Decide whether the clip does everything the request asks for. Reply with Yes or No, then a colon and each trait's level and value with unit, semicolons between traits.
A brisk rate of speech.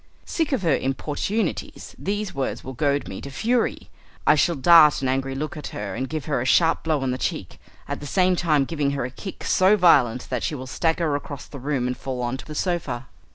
Yes: fast, 230 wpm